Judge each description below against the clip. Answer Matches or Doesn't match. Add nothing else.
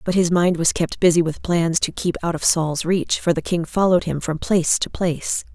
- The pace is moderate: Doesn't match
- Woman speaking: Matches